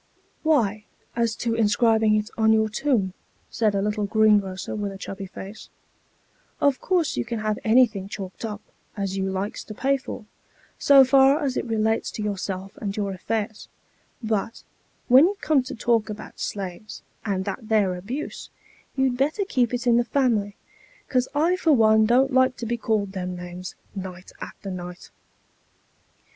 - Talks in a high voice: Yes, high, 220 Hz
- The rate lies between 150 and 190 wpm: Yes, average, 170 wpm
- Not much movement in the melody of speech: No, average, 4.0 semitones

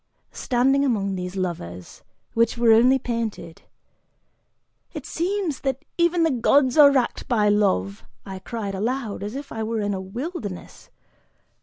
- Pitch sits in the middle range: No, high, 230 Hz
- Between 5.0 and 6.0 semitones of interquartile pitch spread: Yes, wide, 5.4 semitones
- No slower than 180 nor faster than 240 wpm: No, average, 145 wpm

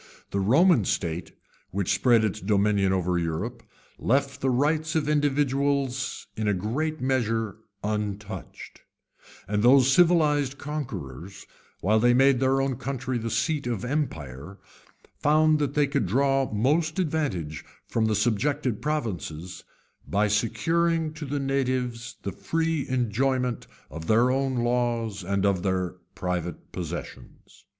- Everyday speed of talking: No, slow, 130 wpm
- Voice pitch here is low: Yes, low, 120 Hz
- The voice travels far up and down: Yes, wide, 5.8 semitones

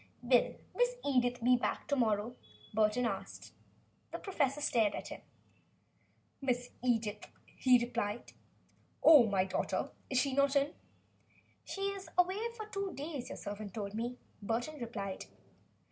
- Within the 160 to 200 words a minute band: No, average, 140 wpm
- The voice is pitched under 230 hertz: No, high, 245 Hz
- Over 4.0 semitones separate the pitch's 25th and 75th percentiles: Yes, average, 4.6 semitones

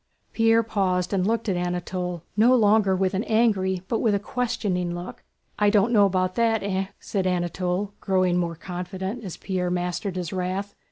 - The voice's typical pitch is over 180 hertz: Yes, high, 190 Hz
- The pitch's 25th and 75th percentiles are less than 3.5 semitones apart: Yes, average, 2.7 semitones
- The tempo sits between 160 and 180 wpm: Yes, average, 175 wpm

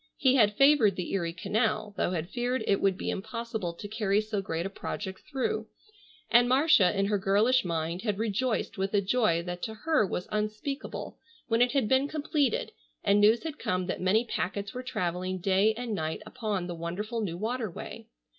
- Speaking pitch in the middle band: No, high, 210 Hz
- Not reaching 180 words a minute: No, average, 195 wpm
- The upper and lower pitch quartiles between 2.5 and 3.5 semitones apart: No, average, 4.5 semitones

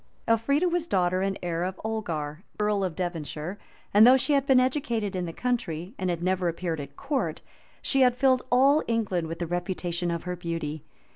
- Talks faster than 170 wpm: Yes, average, 195 wpm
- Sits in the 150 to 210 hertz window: Yes, medium, 185 Hz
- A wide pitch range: Yes, wide, 6.2 semitones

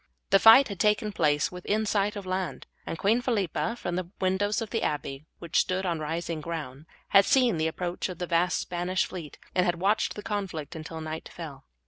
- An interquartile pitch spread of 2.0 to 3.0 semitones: No, average, 4.0 semitones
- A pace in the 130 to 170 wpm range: No, average, 200 wpm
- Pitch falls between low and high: Yes, medium, 180 Hz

